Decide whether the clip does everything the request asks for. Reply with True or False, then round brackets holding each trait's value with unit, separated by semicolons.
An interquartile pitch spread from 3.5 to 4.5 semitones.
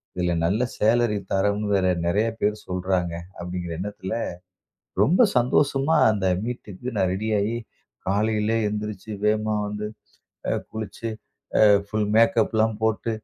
False (2.5 semitones)